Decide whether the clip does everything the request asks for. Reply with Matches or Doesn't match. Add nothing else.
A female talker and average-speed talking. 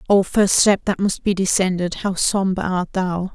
Matches